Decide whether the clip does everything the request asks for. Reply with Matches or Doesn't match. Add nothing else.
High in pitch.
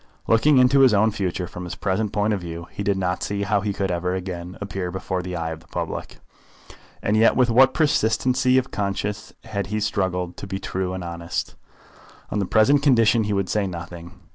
Doesn't match